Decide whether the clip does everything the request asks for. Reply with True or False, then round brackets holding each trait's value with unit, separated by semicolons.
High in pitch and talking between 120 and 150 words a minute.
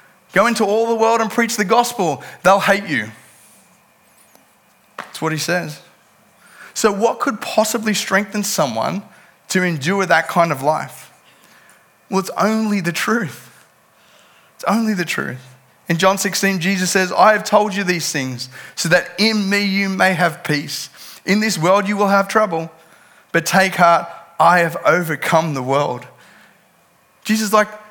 False (195 Hz; 160 wpm)